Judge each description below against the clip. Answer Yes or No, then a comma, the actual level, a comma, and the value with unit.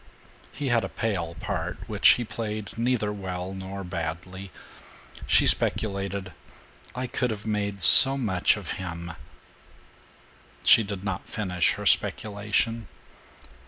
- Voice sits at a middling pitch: No, low, 100 Hz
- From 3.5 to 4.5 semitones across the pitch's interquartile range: No, average, 3.0 semitones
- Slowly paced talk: Yes, slow, 125 wpm